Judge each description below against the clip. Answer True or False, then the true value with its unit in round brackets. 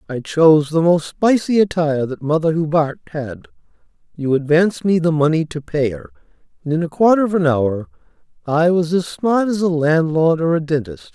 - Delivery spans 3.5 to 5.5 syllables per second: True (5.3 syllables/s)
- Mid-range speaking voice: True (165 Hz)